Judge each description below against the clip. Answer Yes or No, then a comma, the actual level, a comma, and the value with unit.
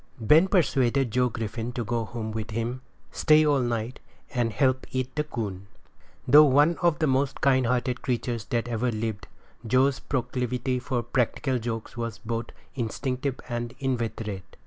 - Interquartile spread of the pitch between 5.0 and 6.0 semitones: No, narrow, 2.5 semitones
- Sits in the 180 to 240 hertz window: No, low, 125 Hz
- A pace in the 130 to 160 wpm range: Yes, average, 155 wpm